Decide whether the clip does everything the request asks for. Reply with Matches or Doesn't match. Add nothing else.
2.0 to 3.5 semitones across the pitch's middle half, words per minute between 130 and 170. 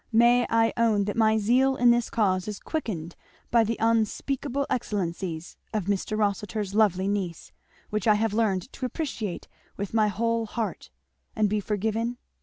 Matches